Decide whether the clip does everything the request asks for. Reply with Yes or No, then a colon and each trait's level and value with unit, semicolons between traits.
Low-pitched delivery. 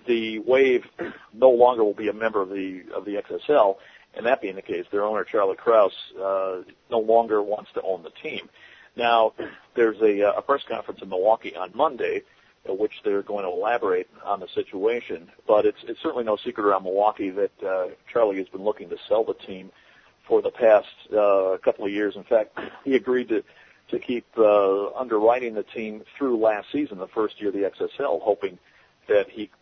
Yes: low, 130 Hz